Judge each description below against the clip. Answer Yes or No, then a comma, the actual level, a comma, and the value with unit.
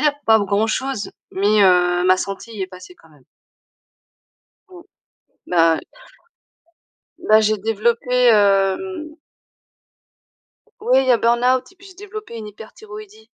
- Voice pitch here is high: Yes, high, 215 Hz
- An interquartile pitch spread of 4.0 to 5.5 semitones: Yes, average, 4.3 semitones